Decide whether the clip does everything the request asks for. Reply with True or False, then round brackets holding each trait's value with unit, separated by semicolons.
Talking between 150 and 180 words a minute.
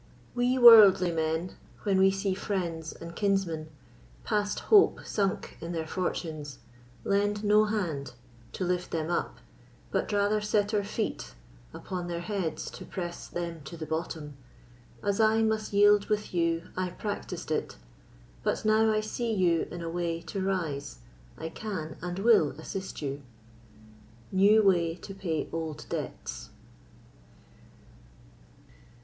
False (140 wpm)